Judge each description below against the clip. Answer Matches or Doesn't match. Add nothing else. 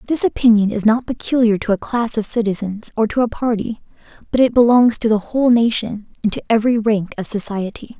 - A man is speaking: Doesn't match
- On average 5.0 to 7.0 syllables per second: Matches